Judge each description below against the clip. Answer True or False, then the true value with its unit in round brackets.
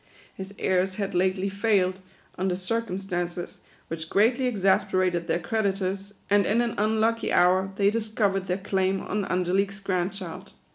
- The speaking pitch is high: True (195 Hz)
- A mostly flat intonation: True (1.9 semitones)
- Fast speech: False (145 wpm)